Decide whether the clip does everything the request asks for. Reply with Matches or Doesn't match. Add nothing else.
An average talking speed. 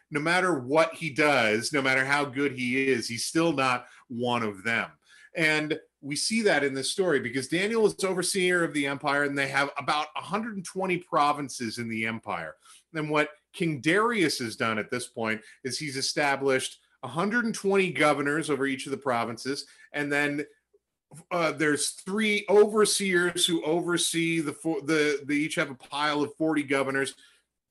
Matches